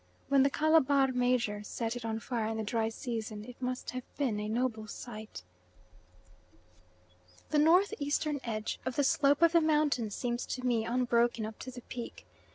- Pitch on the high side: Yes, high, 245 Hz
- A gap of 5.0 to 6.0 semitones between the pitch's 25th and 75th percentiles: No, average, 3.9 semitones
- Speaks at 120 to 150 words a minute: No, average, 175 wpm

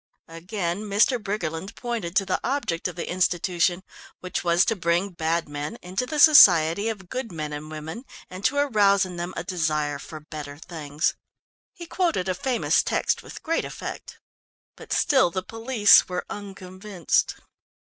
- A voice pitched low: No, medium, 185 Hz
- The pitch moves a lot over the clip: No, average, 4.3 semitones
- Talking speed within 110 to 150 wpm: No, average, 160 wpm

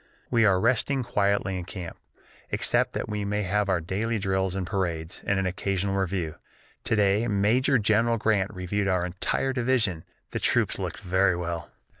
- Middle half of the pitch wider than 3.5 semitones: No, average, 3.1 semitones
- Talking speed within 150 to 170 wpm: Yes, average, 165 wpm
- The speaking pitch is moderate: No, low, 100 Hz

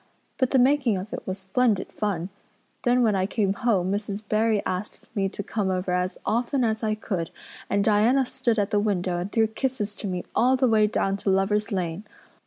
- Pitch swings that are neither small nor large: Yes, average, 3.1 semitones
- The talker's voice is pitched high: Yes, high, 210 Hz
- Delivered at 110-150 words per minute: No, fast, 205 wpm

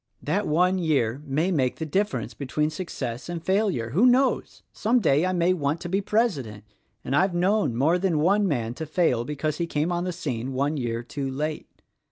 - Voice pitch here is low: No, medium, 155 Hz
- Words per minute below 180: No, fast, 205 wpm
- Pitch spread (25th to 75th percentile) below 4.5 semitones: No, average, 5.3 semitones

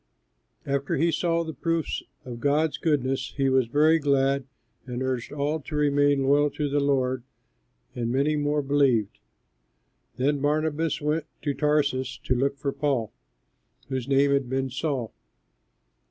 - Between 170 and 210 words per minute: No, average, 145 wpm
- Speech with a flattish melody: Yes, narrow, 2.1 semitones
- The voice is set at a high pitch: No, medium, 140 Hz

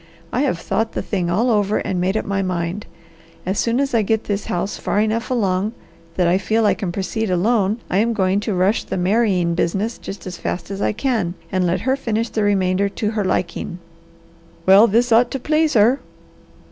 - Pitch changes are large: No, average, 3.4 semitones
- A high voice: Yes, high, 205 Hz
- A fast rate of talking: Yes, fast, 210 wpm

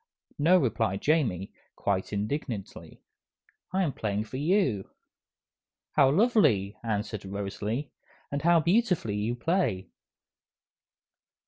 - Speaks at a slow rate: Yes, slow, 95 wpm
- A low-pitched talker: Yes, low, 120 Hz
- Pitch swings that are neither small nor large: No, wide, 8.2 semitones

